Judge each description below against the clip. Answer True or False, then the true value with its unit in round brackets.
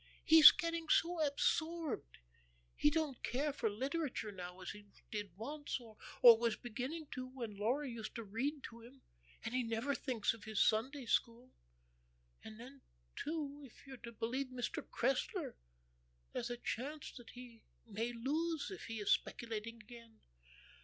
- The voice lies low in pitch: False (245 Hz)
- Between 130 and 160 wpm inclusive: True (155 wpm)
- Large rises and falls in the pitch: False (4.1 semitones)